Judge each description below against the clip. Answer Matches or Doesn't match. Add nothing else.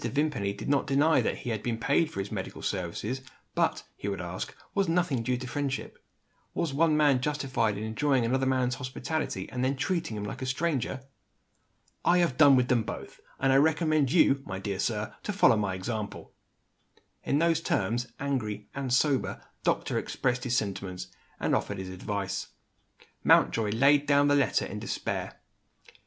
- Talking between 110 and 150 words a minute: Doesn't match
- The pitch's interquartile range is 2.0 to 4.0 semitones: Doesn't match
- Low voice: Matches